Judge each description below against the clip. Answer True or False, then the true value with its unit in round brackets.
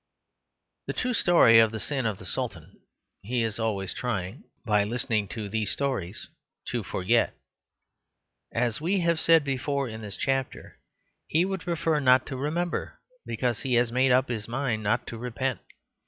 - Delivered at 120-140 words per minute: False (165 wpm)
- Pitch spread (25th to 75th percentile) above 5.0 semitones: False (4.1 semitones)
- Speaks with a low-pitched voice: True (125 Hz)